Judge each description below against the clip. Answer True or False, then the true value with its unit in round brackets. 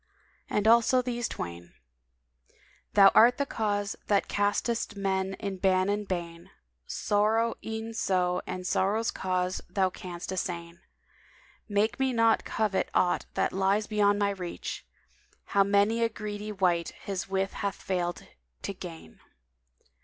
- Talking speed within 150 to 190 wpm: False (140 wpm)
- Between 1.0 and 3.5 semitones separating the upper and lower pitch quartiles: True (2.7 semitones)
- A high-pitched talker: True (200 Hz)